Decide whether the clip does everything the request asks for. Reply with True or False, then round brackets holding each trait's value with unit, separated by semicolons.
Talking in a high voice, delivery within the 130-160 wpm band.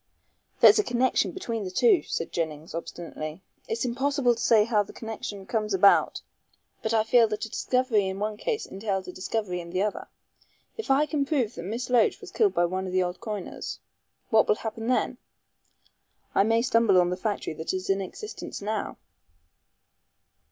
False (215 Hz; 185 wpm)